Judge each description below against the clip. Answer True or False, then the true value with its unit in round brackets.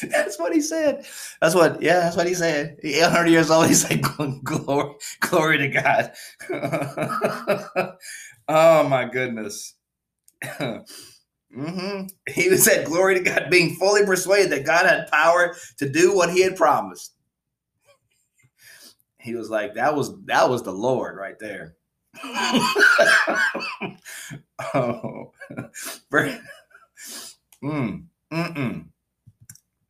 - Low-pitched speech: False (165 Hz)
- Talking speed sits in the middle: False (110 wpm)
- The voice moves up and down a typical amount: True (4.2 semitones)